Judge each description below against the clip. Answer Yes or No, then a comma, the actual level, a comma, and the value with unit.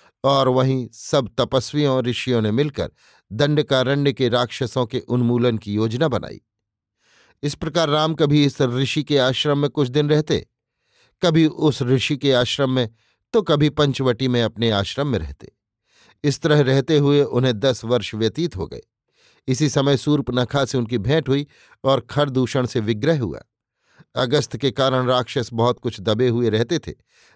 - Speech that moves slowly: No, average, 160 wpm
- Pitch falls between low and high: No, low, 130 Hz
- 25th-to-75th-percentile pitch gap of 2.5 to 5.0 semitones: Yes, average, 3.1 semitones